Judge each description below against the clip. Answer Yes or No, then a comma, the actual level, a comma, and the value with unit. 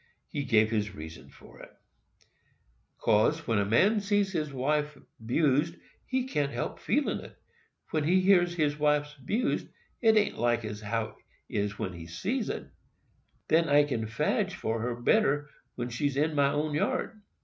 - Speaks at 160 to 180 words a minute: Yes, average, 170 wpm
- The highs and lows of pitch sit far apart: Yes, wide, 6.5 semitones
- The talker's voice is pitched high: No, medium, 145 Hz